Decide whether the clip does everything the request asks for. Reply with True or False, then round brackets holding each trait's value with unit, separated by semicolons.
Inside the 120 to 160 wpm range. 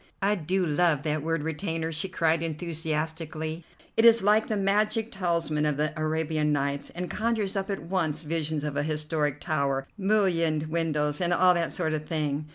False (175 wpm)